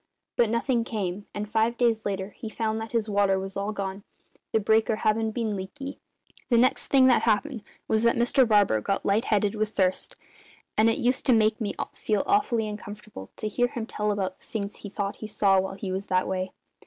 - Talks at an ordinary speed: No, fast, 210 wpm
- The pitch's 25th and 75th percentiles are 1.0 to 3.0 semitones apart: Yes, narrow, 2.5 semitones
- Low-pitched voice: No, high, 215 Hz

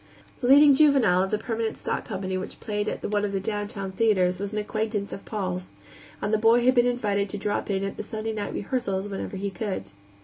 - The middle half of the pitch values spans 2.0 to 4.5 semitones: Yes, narrow, 2.4 semitones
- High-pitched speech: Yes, high, 205 Hz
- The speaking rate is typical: No, fast, 225 wpm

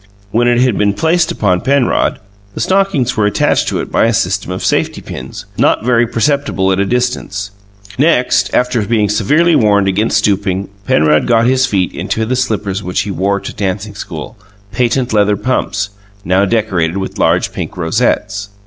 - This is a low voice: Yes, low, 105 Hz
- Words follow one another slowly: No, average, 170 wpm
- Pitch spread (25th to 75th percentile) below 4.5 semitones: Yes, average, 4.1 semitones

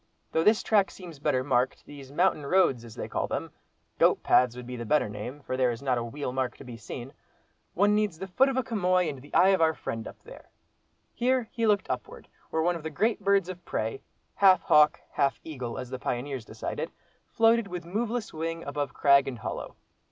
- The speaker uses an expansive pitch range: Yes, wide, 7.0 semitones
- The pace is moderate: No, fast, 210 wpm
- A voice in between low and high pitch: Yes, medium, 150 Hz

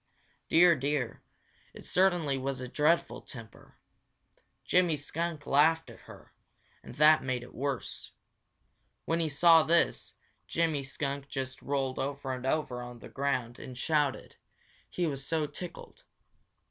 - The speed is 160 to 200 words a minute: No, slow, 135 wpm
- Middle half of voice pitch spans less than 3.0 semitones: No, average, 3.5 semitones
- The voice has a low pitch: No, medium, 145 Hz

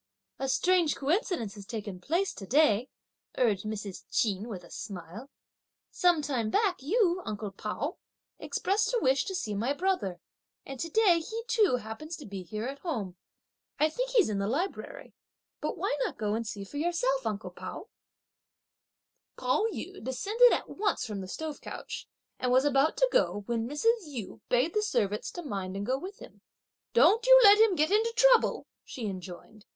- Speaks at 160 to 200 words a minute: Yes, average, 180 wpm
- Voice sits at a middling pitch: No, very high, 270 Hz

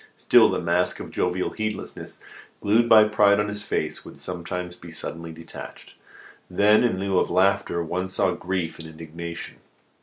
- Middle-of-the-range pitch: No, very low, 90 Hz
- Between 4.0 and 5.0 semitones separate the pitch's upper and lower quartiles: No, average, 3.3 semitones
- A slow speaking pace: No, average, 160 wpm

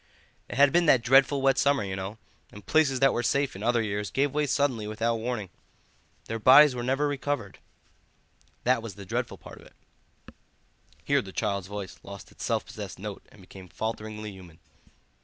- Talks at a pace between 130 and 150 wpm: No, average, 185 wpm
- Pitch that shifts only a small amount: No, average, 5.0 semitones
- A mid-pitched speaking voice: No, low, 115 Hz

